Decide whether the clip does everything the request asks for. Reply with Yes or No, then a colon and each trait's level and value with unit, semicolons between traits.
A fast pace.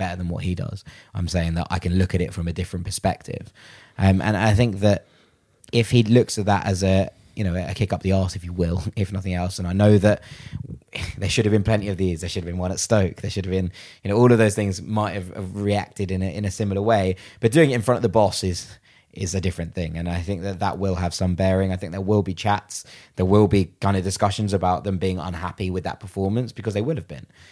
Yes: fast, 275 wpm